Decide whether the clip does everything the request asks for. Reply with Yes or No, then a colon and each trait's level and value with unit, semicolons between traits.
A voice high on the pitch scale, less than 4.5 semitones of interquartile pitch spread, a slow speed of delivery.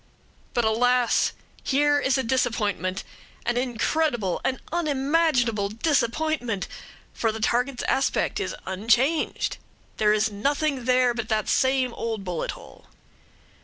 Yes: high, 245 Hz; average, 3.8 semitones; slow, 120 wpm